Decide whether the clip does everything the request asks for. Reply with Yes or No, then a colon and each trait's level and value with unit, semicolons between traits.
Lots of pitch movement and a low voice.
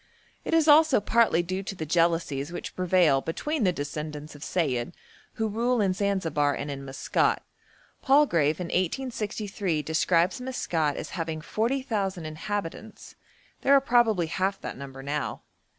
No: wide, 6.0 semitones; medium, 180 Hz